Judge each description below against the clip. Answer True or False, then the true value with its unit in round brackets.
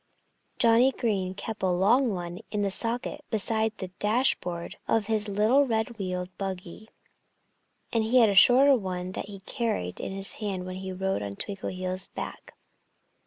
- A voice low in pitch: False (200 Hz)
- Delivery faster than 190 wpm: False (165 wpm)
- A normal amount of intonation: True (3.5 semitones)